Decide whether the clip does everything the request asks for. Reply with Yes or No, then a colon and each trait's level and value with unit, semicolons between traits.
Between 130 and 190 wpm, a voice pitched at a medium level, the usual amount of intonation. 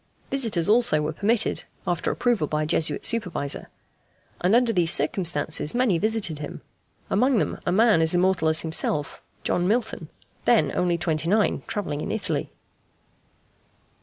No: average, 145 wpm; medium, 180 Hz; wide, 5.7 semitones